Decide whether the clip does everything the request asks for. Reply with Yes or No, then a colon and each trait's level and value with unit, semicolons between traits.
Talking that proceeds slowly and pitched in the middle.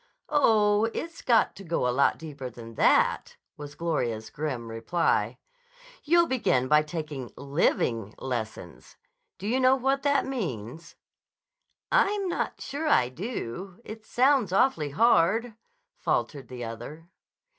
Yes: slow, 130 wpm; medium, 165 Hz